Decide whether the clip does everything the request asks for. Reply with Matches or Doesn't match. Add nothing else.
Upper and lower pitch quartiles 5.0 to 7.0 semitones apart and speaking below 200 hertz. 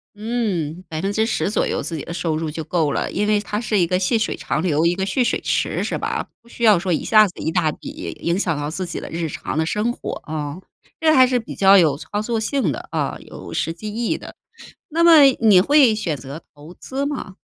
Matches